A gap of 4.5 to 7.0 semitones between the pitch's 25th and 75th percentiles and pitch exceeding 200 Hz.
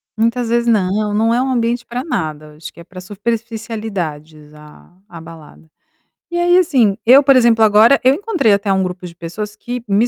Yes: average, 5.0 semitones; high, 215 Hz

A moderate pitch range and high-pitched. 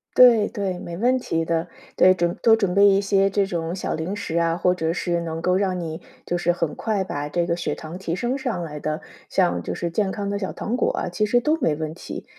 No: average, 3.3 semitones; medium, 180 Hz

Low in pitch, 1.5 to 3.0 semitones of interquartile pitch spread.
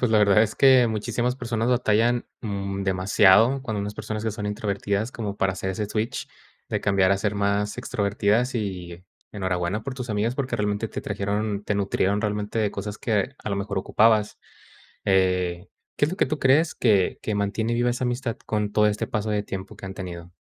Yes: low, 105 Hz; narrow, 2.5 semitones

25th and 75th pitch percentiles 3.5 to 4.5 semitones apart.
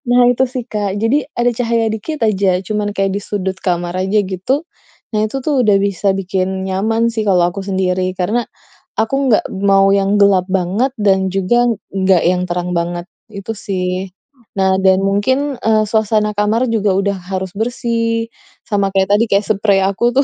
No: average, 2.9 semitones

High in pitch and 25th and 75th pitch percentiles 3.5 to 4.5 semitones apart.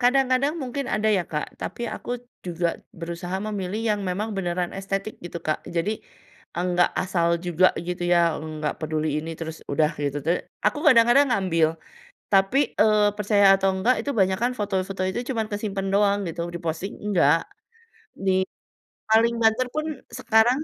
Yes: high, 195 Hz; average, 4.1 semitones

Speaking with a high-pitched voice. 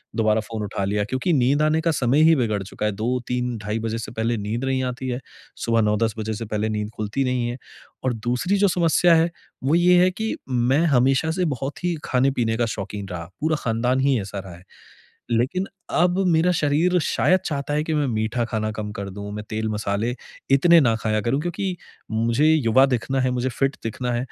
No: low, 125 Hz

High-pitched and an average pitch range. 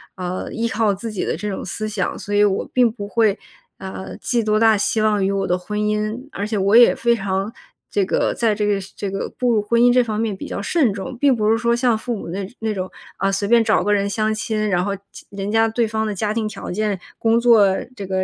No: high, 215 Hz; narrow, 2.2 semitones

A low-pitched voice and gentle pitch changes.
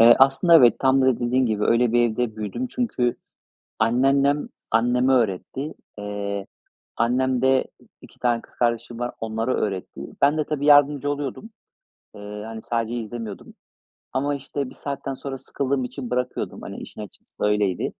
No: low, 125 Hz; average, 3.4 semitones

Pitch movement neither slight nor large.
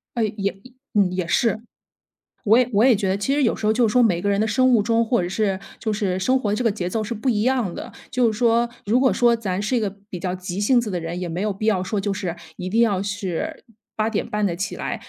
Yes: average, 3.4 semitones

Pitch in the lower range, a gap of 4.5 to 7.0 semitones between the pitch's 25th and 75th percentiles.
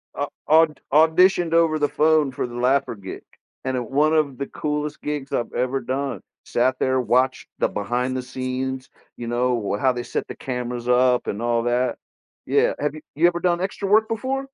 No: low, 130 Hz; average, 3.8 semitones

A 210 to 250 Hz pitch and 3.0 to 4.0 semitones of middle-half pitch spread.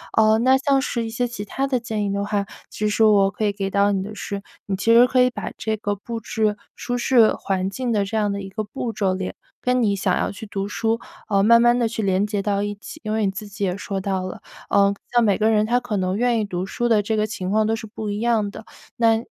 No: high, 215 Hz; narrow, 2.4 semitones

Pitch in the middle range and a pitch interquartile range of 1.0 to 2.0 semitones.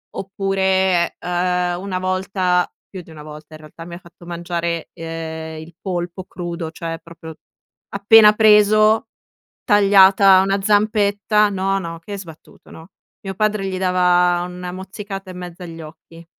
No: medium, 180 Hz; narrow, 2.5 semitones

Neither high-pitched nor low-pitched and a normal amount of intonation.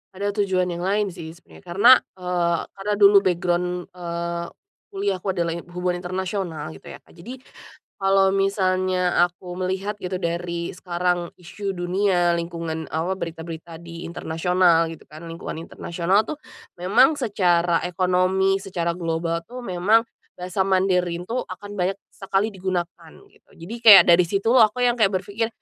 No: medium, 180 Hz; narrow, 2.3 semitones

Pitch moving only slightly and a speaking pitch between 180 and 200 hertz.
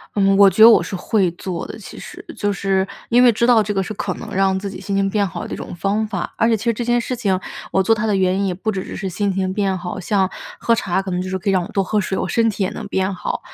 Yes: narrow, 2.3 semitones; high, 195 Hz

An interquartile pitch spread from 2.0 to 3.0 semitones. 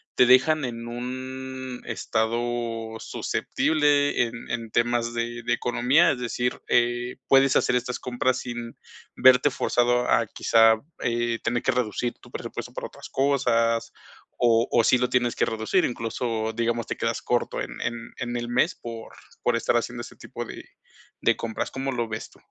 No: narrow, 1.4 semitones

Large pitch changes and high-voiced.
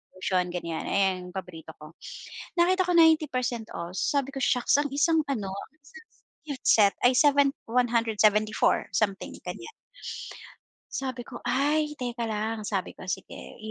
Yes: wide, 6.2 semitones; high, 235 Hz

